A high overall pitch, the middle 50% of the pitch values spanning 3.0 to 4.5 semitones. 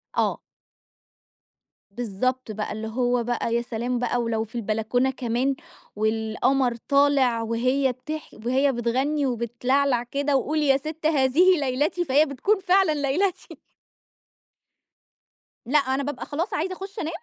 Yes: very high, 260 Hz; average, 3.6 semitones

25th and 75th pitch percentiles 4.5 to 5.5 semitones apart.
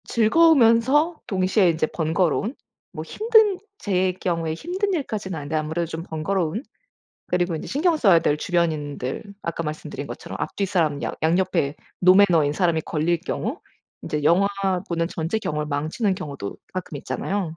Yes: average, 5.2 semitones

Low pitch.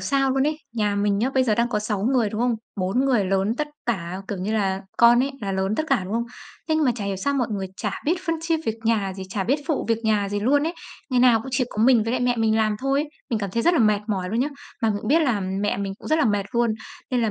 No: high, 225 Hz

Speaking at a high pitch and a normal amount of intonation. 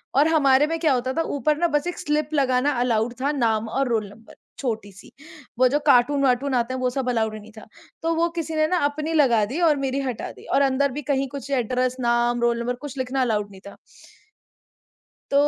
Yes: very high, 260 Hz; average, 3.4 semitones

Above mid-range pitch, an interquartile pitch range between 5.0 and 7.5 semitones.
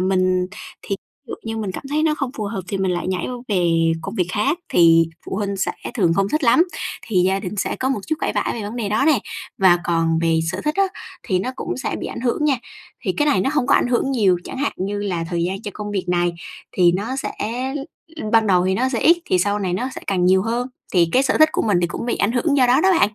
Yes: high, 205 Hz; wide, 5.5 semitones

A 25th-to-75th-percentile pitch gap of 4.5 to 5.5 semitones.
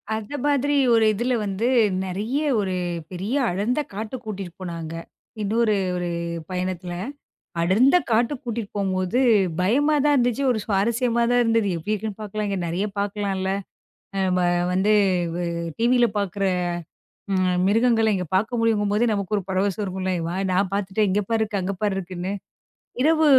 No: average, 3.8 semitones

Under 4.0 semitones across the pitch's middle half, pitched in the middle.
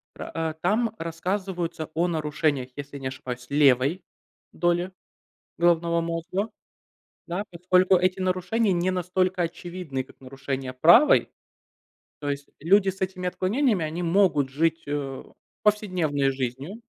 No: average, 4.4 semitones; medium, 170 Hz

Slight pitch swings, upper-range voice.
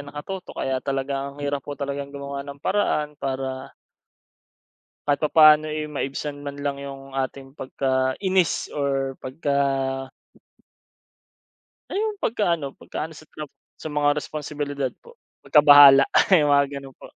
No: narrow, 1.7 semitones; medium, 140 Hz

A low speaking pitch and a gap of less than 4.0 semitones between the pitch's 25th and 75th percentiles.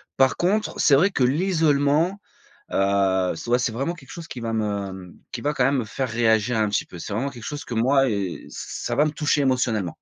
No: low, 125 Hz; average, 5.1 semitones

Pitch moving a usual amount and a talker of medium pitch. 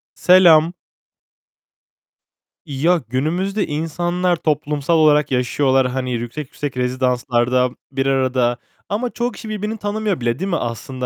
No: wide, 5.8 semitones; medium, 150 Hz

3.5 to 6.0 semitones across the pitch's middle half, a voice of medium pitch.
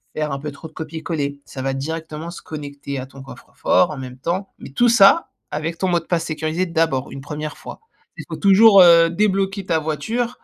Yes: average, 4.1 semitones; medium, 160 Hz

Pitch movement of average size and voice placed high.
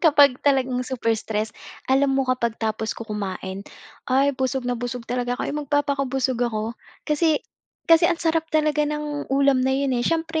Yes: average, 3.4 semitones; very high, 265 Hz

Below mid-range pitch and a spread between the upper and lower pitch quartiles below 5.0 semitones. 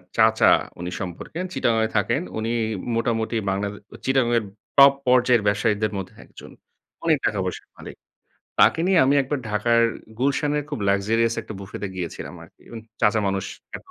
Yes: low, 115 Hz; average, 3.9 semitones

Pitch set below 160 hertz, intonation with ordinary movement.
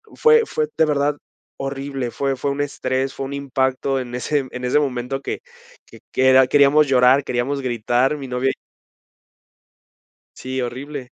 No: low, 135 Hz; narrow, 1.9 semitones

